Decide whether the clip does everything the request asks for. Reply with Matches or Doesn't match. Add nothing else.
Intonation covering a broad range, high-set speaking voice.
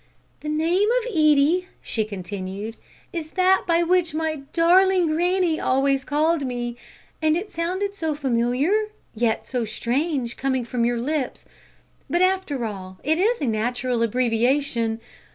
Matches